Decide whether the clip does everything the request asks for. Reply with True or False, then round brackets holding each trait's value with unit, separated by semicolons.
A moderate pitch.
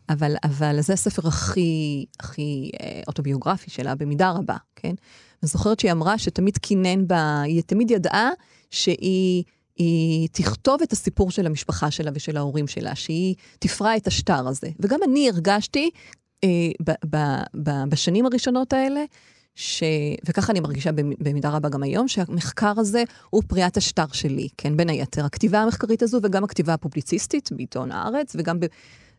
True (175 Hz)